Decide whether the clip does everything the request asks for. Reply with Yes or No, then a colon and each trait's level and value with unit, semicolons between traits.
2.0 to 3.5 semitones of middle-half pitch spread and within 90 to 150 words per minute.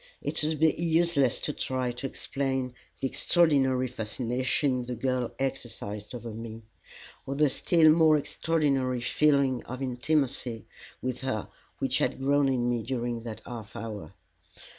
Yes: average, 2.9 semitones; average, 140 wpm